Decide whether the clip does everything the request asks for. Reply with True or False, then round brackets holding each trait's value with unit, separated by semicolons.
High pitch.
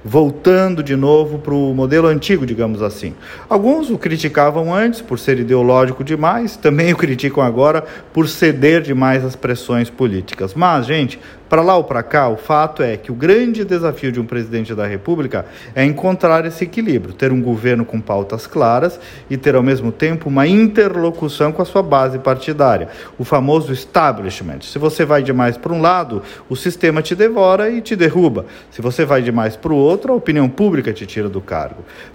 False (145 Hz)